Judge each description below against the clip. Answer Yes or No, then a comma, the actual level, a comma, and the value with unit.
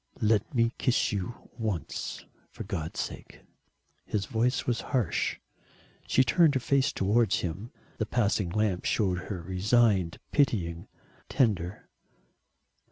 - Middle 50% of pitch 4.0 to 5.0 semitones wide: Yes, average, 4.5 semitones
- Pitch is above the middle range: No, low, 105 Hz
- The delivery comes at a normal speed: No, slow, 120 wpm